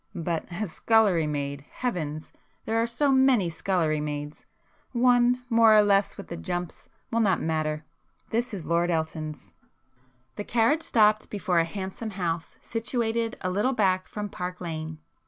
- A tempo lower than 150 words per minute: Yes, average, 140 wpm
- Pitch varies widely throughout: Yes, wide, 5.7 semitones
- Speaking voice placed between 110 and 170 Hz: No, high, 190 Hz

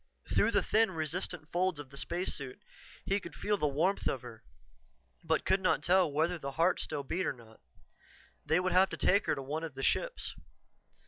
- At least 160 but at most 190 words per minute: No, average, 200 wpm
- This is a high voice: No, medium, 165 Hz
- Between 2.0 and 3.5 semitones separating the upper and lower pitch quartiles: No, average, 4.8 semitones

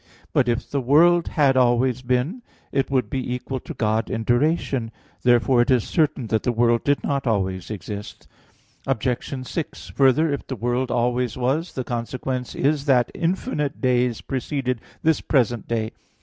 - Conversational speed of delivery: Yes, average, 165 wpm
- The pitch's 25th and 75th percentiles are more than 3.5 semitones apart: No, average, 2.7 semitones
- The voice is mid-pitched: No, low, 125 Hz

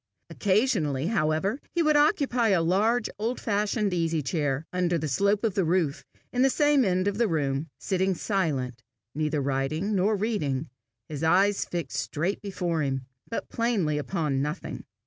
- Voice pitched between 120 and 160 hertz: No, medium, 180 Hz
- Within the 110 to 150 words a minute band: No, average, 160 wpm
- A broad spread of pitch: Yes, wide, 5.7 semitones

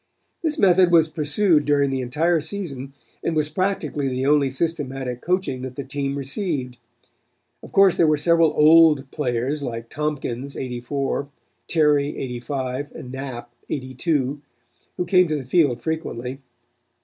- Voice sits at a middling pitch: Yes, medium, 145 Hz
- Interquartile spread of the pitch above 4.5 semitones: No, average, 3.7 semitones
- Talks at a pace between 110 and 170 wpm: Yes, average, 140 wpm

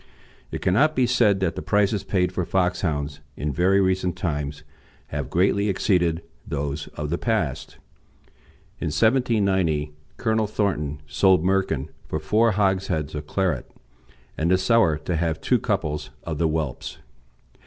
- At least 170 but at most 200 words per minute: No, average, 145 wpm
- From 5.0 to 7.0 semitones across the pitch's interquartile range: No, average, 4.6 semitones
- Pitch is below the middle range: Yes, very low, 90 Hz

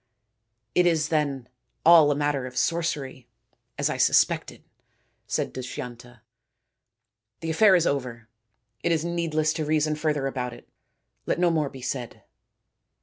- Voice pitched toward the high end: No, medium, 145 Hz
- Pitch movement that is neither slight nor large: Yes, average, 4.5 semitones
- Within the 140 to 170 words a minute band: Yes, average, 150 wpm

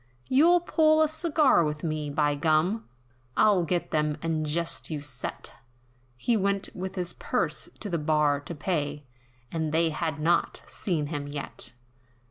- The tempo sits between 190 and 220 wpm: No, average, 155 wpm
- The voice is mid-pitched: Yes, medium, 160 Hz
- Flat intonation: No, average, 4.3 semitones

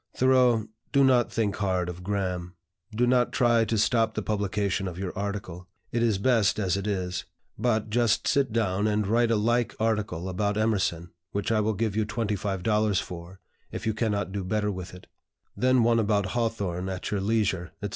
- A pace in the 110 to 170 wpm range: No, average, 185 wpm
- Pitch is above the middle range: No, low, 105 Hz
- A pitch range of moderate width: Yes, average, 3.0 semitones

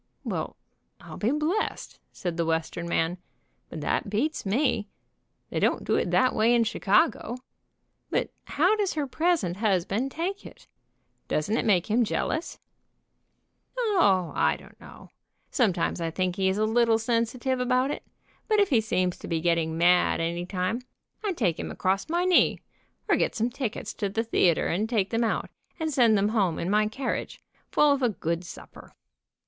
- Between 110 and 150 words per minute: No, average, 175 wpm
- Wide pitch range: Yes, wide, 6.2 semitones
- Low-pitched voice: No, high, 220 Hz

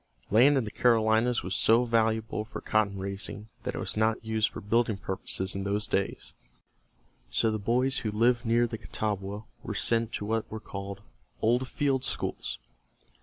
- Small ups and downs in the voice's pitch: Yes, narrow, 2.3 semitones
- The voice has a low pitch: Yes, low, 110 Hz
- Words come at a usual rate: Yes, average, 170 wpm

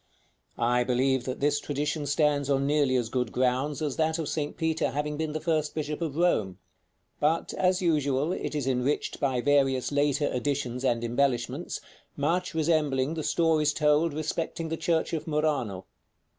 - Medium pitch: Yes, medium, 145 Hz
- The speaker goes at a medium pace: Yes, average, 165 wpm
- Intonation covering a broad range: No, average, 3.0 semitones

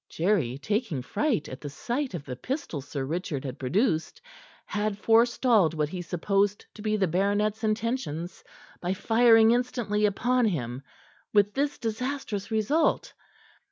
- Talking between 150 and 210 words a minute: No, average, 140 wpm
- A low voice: No, high, 205 Hz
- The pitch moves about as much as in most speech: No, wide, 6.0 semitones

